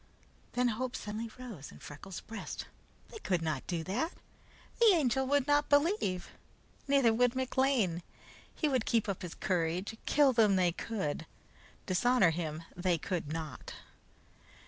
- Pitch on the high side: Yes, high, 220 Hz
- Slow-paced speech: No, average, 145 wpm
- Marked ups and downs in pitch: Yes, wide, 6.8 semitones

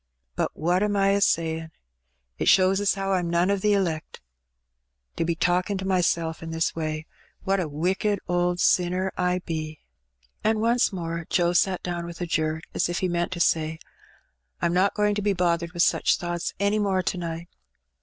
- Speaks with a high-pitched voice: No, medium, 175 Hz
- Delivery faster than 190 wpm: Yes, average, 200 wpm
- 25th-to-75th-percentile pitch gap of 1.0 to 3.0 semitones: Yes, narrow, 2.6 semitones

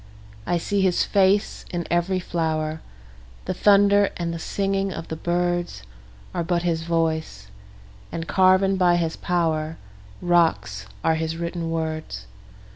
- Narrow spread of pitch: Yes, narrow, 2.3 semitones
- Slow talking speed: Yes, slow, 120 wpm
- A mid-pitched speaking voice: Yes, medium, 165 Hz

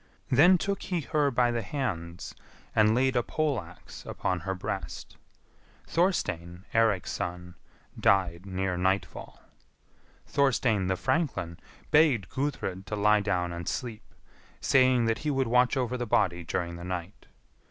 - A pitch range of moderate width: No, wide, 6.5 semitones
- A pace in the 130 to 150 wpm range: Yes, average, 140 wpm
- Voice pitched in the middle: No, low, 105 Hz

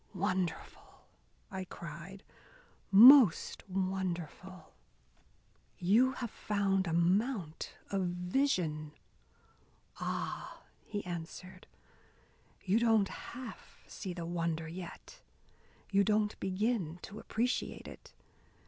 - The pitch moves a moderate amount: Yes, average, 3.5 semitones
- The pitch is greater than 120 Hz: Yes, high, 190 Hz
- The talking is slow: Yes, slow, 90 wpm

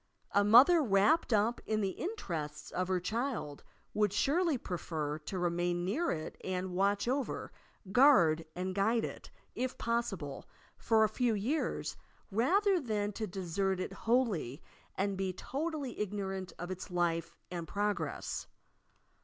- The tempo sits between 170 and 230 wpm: No, average, 145 wpm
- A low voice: No, high, 200 Hz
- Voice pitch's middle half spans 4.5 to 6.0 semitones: Yes, average, 5.0 semitones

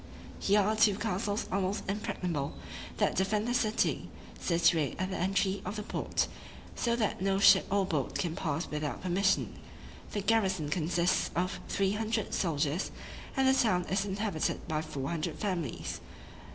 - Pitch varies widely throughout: No, average, 3.5 semitones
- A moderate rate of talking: Yes, average, 155 wpm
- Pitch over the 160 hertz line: Yes, high, 190 Hz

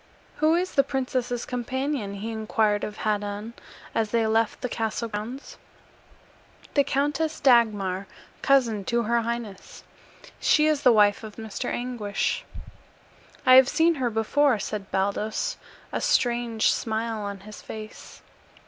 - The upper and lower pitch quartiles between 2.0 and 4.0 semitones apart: Yes, average, 3.4 semitones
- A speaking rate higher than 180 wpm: No, slow, 135 wpm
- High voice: Yes, high, 230 Hz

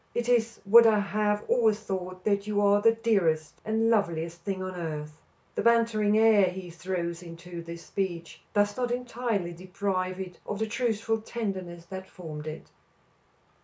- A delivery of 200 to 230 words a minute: No, average, 165 wpm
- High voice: Yes, high, 200 Hz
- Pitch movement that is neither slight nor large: Yes, average, 4.1 semitones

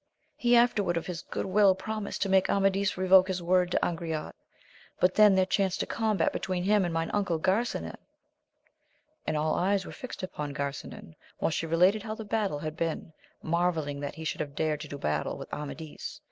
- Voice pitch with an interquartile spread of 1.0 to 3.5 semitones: No, average, 3.9 semitones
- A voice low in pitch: No, medium, 185 Hz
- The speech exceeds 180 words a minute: Yes, average, 190 wpm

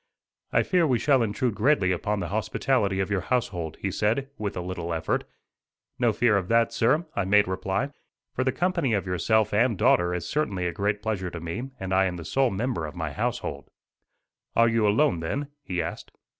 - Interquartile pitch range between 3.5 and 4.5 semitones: No, average, 5.0 semitones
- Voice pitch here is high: No, low, 105 Hz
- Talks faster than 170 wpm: Yes, average, 200 wpm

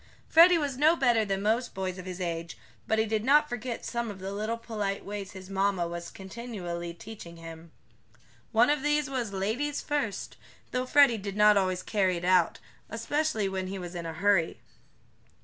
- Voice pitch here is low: No, high, 205 Hz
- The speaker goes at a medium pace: Yes, average, 185 wpm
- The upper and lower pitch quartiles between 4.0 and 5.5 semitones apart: Yes, average, 4.6 semitones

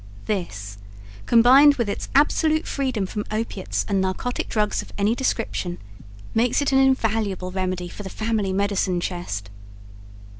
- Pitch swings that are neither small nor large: Yes, average, 4.7 semitones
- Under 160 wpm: Yes, average, 140 wpm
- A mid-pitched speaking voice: No, high, 210 Hz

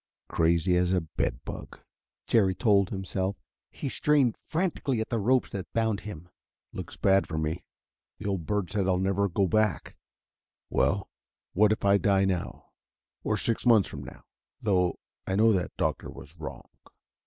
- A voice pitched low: Yes, low, 100 Hz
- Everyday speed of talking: Yes, average, 165 wpm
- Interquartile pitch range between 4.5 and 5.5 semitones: No, average, 3.2 semitones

